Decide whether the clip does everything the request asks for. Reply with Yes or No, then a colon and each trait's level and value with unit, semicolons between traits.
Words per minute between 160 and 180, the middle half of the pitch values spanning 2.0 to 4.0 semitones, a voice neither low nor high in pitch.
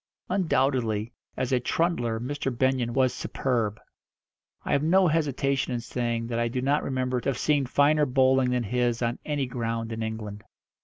No: average, 170 wpm; average, 2.8 semitones; low, 125 Hz